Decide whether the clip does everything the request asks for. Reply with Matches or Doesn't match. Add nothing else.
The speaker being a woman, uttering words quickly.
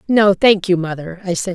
Matches